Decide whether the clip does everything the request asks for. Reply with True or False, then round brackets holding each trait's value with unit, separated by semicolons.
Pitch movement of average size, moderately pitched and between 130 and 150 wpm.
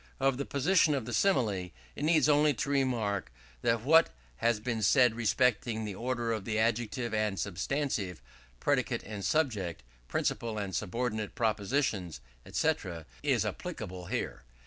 False (4.4 semitones; 115 Hz; 145 wpm)